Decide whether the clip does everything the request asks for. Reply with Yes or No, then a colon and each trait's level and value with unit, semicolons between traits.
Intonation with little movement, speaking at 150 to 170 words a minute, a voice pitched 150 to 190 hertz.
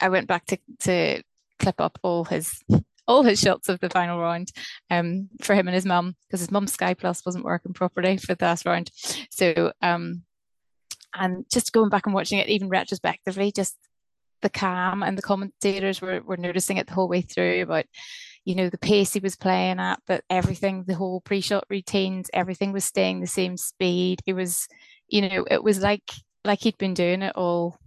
No: narrow, 1.9 semitones; average, 200 wpm; medium, 185 Hz